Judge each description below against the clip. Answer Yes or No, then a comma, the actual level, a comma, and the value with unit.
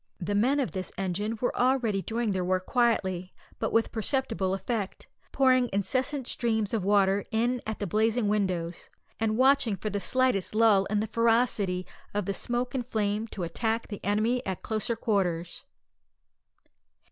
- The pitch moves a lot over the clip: No, average, 3.5 semitones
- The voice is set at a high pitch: Yes, high, 215 Hz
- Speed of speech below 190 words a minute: Yes, average, 160 wpm